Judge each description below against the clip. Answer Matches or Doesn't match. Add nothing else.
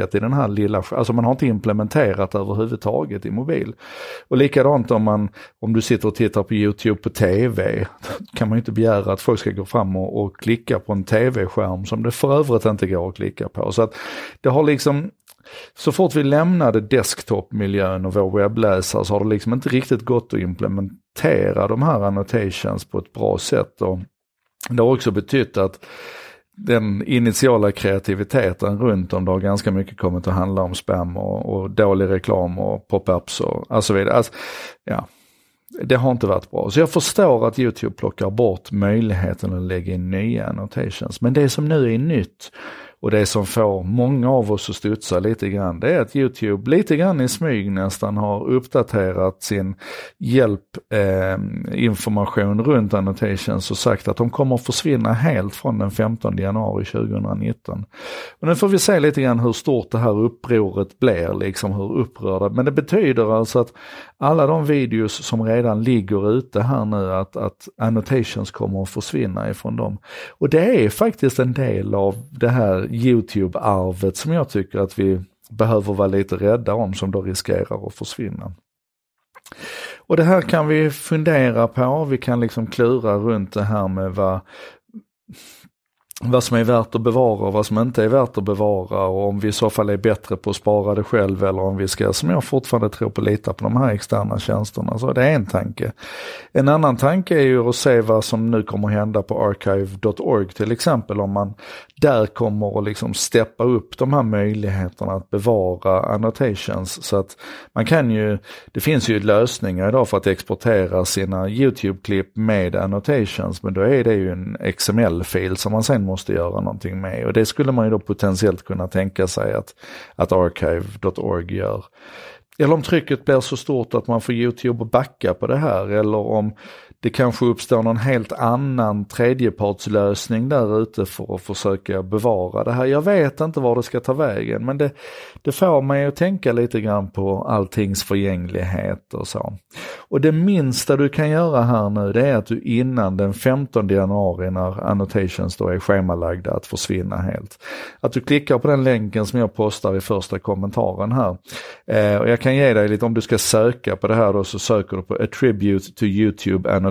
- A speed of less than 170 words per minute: Doesn't match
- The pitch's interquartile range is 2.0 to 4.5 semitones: Matches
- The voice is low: Matches